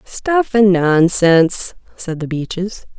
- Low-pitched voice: No, high, 190 Hz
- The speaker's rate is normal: No, slow, 120 wpm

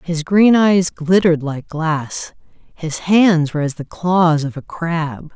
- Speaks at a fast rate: No, average, 170 wpm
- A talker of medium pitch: Yes, medium, 165 Hz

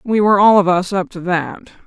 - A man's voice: No, female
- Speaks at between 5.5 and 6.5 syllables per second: Yes, 5.9 syllables/s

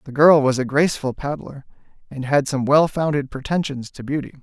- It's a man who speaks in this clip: Yes, male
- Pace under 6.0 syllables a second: Yes, 5.5 syllables/s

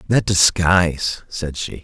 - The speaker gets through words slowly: Yes, slow, 130 wpm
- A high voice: No, very low, 90 Hz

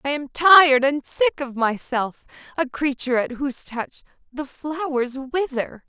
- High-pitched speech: Yes, very high, 275 Hz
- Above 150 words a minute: No, average, 145 wpm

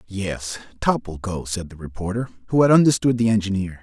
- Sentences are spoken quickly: No, average, 190 wpm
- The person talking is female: No, male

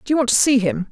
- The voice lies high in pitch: Yes, high, 245 Hz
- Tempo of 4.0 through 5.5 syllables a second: No, 7.4 syllables/s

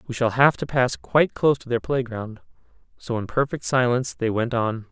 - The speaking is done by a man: Yes, male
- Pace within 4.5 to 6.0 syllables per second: Yes, 5.5 syllables/s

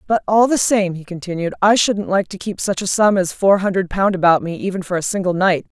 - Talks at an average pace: No, fast, 260 wpm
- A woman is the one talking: Yes, female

